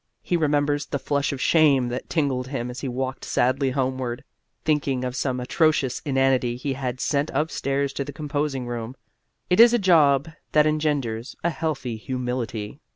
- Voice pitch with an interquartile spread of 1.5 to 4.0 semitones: Yes, average, 2.8 semitones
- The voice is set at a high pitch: No, low, 135 Hz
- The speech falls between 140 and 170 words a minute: Yes, average, 165 wpm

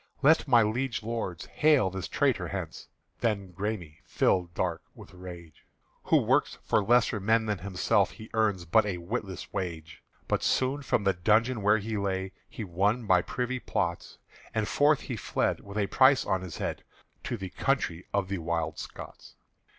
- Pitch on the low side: Yes, low, 100 Hz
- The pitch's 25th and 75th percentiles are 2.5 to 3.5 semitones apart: No, average, 3.9 semitones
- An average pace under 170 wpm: No, average, 175 wpm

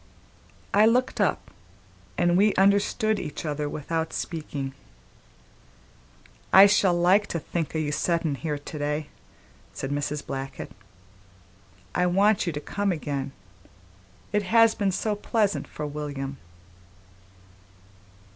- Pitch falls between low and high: Yes, medium, 170 Hz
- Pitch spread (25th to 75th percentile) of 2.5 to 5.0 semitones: No, wide, 5.4 semitones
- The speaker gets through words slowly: Yes, slow, 120 wpm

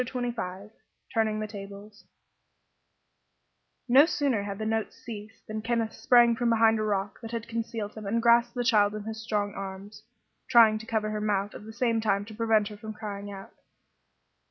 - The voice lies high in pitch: Yes, high, 220 Hz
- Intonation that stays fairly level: Yes, narrow, 2.0 semitones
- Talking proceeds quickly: No, average, 185 wpm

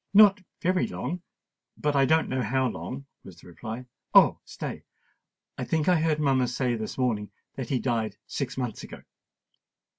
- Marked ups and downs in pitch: No, average, 4.5 semitones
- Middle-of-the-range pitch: No, low, 130 Hz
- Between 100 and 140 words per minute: No, average, 155 wpm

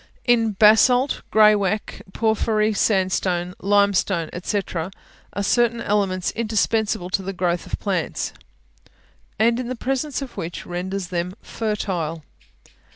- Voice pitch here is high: Yes, high, 205 Hz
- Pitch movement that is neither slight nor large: Yes, average, 3.4 semitones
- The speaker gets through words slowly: Yes, slow, 110 wpm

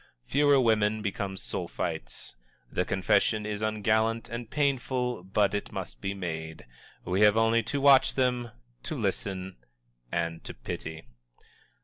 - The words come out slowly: Yes, slow, 130 wpm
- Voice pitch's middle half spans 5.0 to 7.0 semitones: No, average, 4.2 semitones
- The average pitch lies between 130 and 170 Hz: No, low, 105 Hz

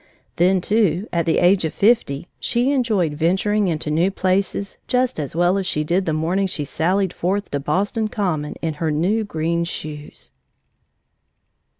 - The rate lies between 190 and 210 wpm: No, average, 165 wpm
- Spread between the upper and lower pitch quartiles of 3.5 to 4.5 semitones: Yes, average, 3.9 semitones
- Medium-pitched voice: Yes, medium, 180 Hz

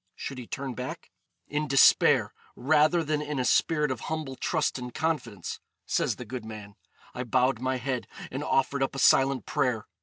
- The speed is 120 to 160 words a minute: No, average, 180 wpm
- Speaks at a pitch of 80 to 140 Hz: Yes, low, 135 Hz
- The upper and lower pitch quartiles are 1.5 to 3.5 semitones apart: Yes, average, 2.9 semitones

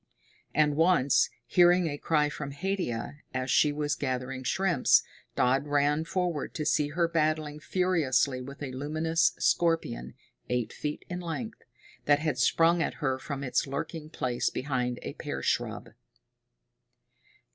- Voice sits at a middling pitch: Yes, medium, 150 Hz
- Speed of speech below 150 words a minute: Yes, average, 140 wpm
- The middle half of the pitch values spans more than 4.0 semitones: No, average, 3.7 semitones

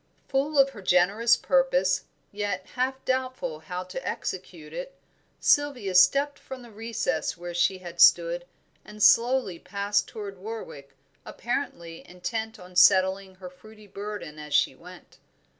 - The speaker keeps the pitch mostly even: No, average, 5.3 semitones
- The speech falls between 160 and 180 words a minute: No, average, 140 wpm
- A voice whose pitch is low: No, high, 200 Hz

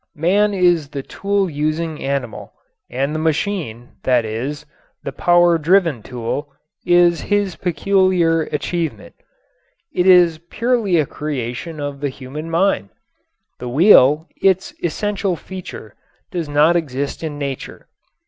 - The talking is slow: Yes, slow, 125 wpm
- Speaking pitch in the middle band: Yes, medium, 160 Hz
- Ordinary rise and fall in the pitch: Yes, average, 4.1 semitones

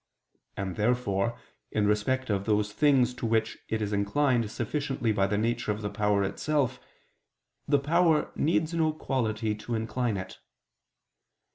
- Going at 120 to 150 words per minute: Yes, average, 145 wpm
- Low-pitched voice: Yes, low, 115 Hz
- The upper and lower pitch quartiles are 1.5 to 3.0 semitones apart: No, average, 4.3 semitones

